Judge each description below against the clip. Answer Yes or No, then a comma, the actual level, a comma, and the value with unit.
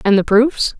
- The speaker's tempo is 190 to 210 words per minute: No, fast, 225 wpm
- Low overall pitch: No, high, 230 Hz